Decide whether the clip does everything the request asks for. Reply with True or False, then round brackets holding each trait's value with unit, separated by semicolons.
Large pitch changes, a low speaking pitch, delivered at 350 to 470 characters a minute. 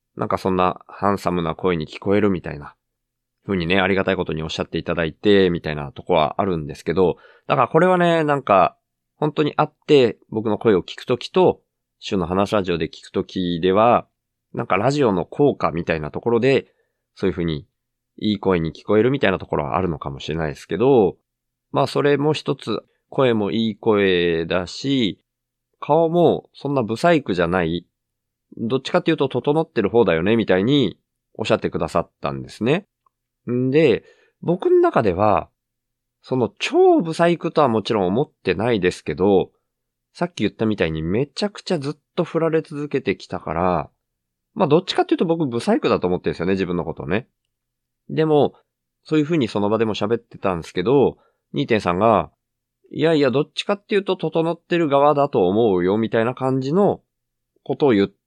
True (9.0 semitones; 110 Hz; 370 characters per minute)